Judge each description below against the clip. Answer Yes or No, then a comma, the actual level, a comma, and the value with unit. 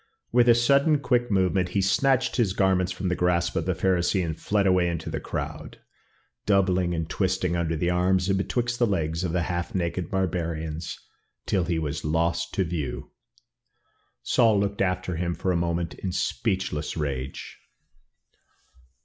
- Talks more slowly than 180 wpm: Yes, average, 165 wpm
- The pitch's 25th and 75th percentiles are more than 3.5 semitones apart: No, narrow, 2.5 semitones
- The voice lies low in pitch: Yes, very low, 90 Hz